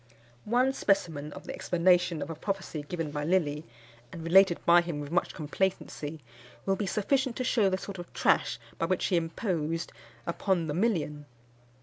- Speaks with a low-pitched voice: No, medium, 175 Hz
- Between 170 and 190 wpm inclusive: Yes, average, 175 wpm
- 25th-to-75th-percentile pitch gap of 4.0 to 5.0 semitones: No, average, 3.5 semitones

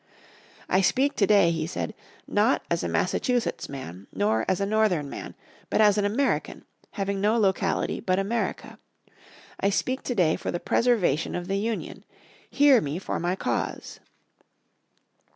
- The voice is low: No, high, 195 Hz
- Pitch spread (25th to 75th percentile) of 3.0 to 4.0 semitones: No, average, 4.4 semitones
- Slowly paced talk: No, average, 150 wpm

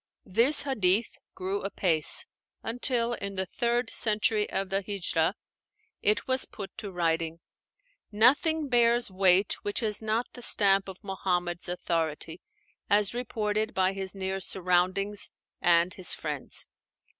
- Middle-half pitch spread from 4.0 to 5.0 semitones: No, average, 3.6 semitones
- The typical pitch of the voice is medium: No, high, 195 Hz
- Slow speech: Yes, slow, 130 wpm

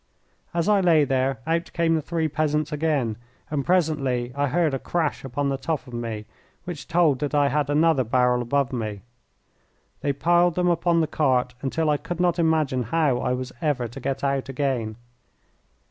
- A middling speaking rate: Yes, average, 185 wpm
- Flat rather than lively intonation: No, average, 4.0 semitones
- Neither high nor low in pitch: Yes, medium, 145 Hz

